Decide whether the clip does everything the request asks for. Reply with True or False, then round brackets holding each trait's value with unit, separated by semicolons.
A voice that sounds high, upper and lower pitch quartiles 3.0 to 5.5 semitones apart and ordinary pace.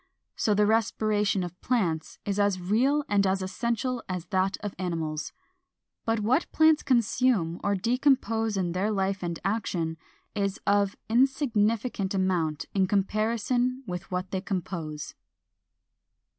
False (205 Hz; 3.7 semitones; 130 wpm)